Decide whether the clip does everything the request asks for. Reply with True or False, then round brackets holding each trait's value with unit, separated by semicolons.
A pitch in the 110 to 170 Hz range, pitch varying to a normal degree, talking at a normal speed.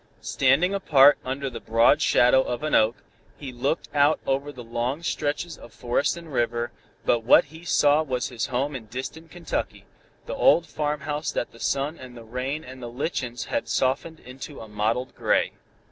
True (135 Hz; 3.6 semitones; 175 wpm)